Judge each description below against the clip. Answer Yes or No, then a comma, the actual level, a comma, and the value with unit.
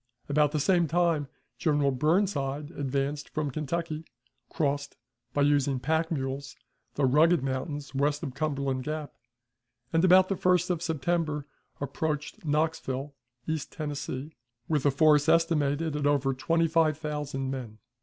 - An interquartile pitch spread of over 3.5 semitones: No, narrow, 2.6 semitones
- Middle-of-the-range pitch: Yes, medium, 150 Hz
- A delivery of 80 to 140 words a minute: Yes, slow, 135 wpm